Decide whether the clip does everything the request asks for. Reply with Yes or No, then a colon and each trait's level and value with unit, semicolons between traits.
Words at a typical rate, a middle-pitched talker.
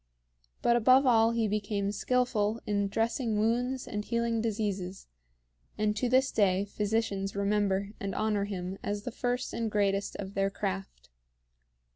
No: average, 145 wpm; high, 210 Hz